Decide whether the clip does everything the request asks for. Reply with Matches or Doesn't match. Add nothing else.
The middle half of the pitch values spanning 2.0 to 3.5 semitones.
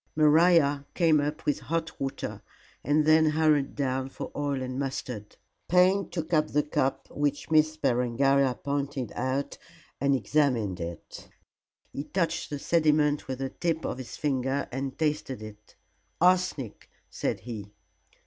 Matches